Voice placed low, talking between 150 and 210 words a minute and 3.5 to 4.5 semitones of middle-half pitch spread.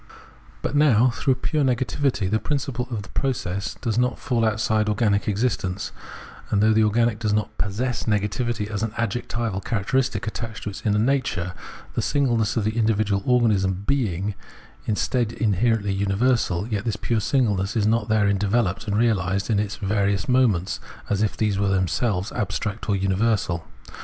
No: low, 110 Hz; average, 160 wpm; average, 3.0 semitones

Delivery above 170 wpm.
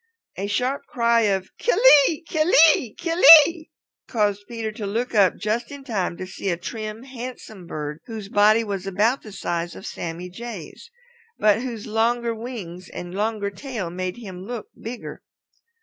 No: average, 165 wpm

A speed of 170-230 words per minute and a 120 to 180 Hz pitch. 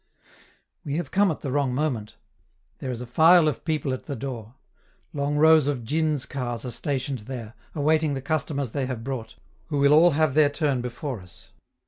Yes: average, 190 wpm; medium, 140 Hz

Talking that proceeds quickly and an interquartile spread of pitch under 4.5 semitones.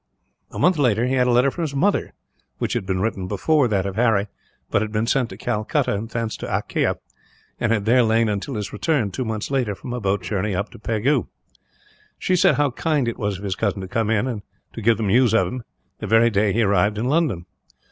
Yes: fast, 235 wpm; average, 3.6 semitones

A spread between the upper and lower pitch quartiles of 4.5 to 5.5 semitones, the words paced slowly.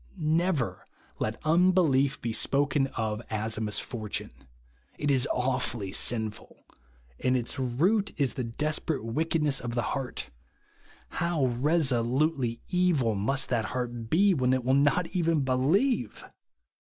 Yes: average, 4.8 semitones; slow, 125 wpm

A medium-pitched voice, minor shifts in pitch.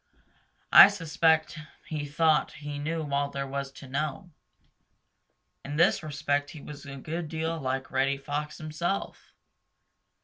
Yes: medium, 150 Hz; narrow, 2.2 semitones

